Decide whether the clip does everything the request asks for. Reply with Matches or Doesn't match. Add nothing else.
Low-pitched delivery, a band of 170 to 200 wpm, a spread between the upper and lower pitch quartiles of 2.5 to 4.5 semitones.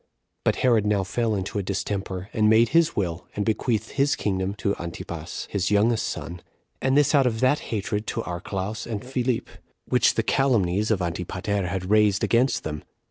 Matches